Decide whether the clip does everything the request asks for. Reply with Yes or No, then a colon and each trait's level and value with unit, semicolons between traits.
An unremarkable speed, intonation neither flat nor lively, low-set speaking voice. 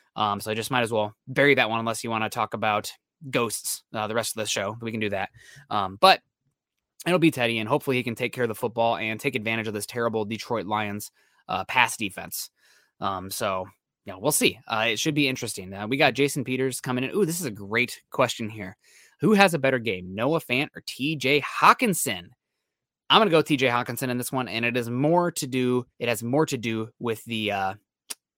No: fast, 230 wpm; average, 3.7 semitones; low, 120 Hz